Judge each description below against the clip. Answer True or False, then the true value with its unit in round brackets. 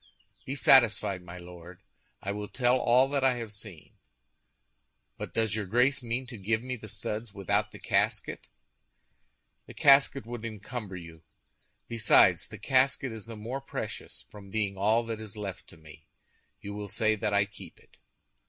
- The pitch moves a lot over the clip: False (3.5 semitones)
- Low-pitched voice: True (110 Hz)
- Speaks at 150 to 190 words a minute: True (170 wpm)